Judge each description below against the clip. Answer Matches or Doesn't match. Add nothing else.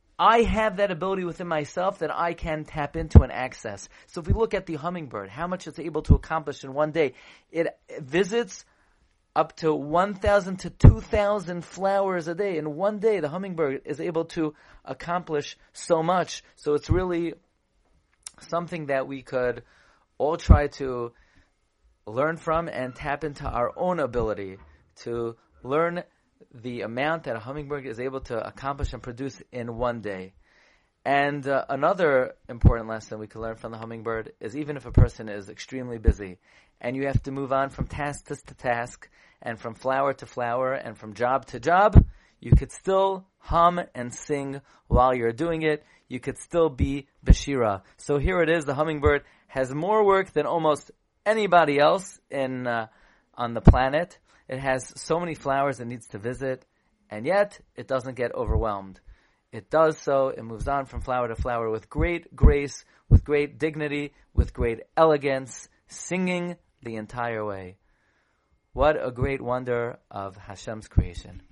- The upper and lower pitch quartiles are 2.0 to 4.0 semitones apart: Doesn't match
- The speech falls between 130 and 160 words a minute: Doesn't match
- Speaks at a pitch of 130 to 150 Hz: Matches